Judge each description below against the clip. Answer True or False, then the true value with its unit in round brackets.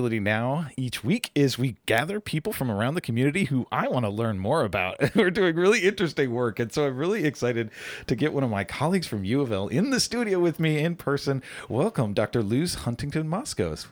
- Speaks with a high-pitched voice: False (140 Hz)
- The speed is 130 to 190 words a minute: False (205 wpm)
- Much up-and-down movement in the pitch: True (5.8 semitones)